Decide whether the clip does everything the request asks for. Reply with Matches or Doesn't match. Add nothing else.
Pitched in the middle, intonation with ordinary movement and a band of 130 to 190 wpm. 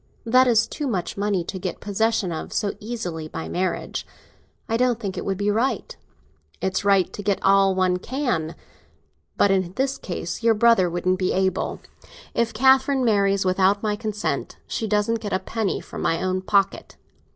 Doesn't match